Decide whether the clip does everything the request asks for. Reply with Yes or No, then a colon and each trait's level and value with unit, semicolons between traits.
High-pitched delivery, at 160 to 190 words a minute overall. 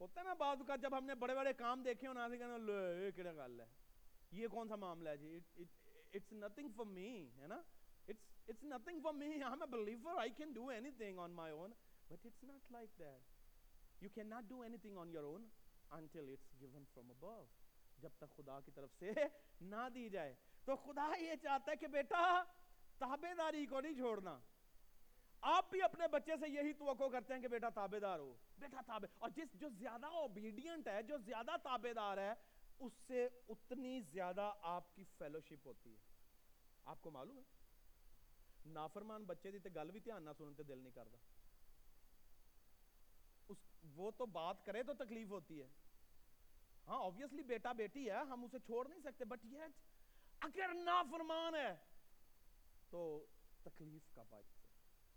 Yes: high, 220 Hz; average, 175 wpm